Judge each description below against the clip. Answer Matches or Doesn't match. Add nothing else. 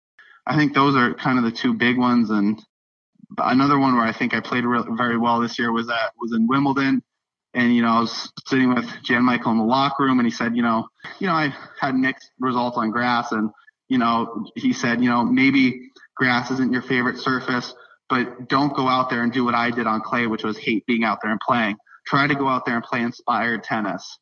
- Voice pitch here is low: Matches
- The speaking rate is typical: Doesn't match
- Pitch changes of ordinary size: Doesn't match